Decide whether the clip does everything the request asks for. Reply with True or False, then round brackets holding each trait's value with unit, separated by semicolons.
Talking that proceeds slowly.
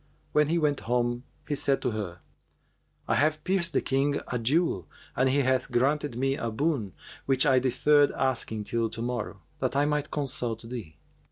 False (180 wpm)